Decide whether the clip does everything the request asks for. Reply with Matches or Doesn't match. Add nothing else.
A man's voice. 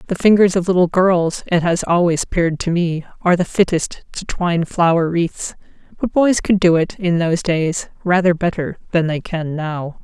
Doesn't match